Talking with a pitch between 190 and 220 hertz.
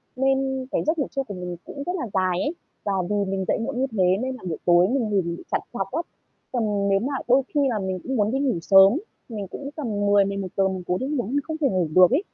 Yes: high, 210 Hz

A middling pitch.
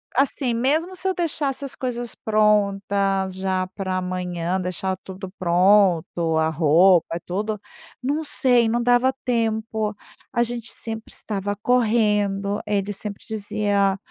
No: high, 205 Hz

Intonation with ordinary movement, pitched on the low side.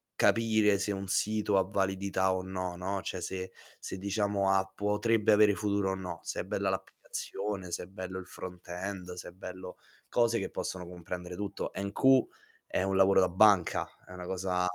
No: narrow, 1.8 semitones; very low, 95 Hz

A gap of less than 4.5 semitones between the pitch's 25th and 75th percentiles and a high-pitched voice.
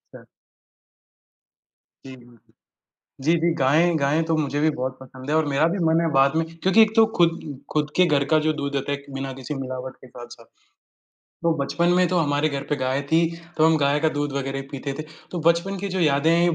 No: average, 3.3 semitones; medium, 150 Hz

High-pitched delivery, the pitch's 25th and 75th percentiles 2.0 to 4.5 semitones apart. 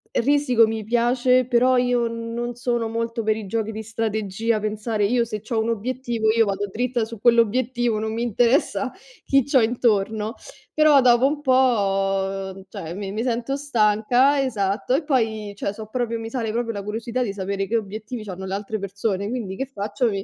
Yes: high, 225 Hz; average, 2.7 semitones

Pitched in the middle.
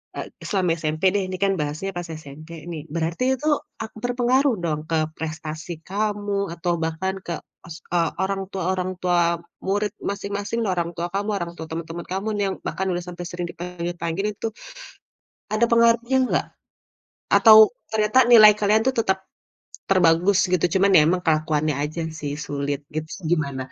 Yes: medium, 180 Hz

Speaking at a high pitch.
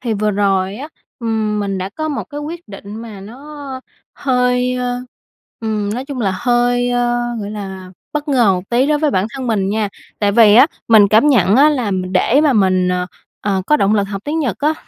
Yes: high, 225 Hz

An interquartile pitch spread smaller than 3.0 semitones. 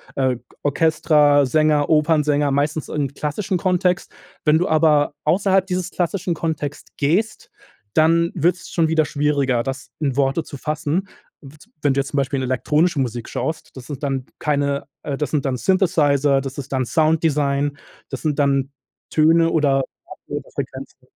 Yes: narrow, 2.6 semitones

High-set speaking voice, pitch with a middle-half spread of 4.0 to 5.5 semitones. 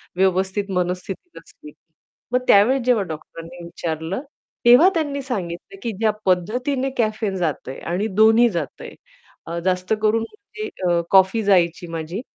Yes: high, 195 Hz; average, 5.2 semitones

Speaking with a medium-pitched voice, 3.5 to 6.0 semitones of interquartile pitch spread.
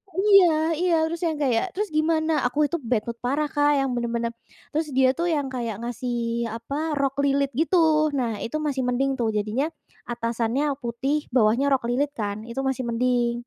No: very high, 265 Hz; average, 4.1 semitones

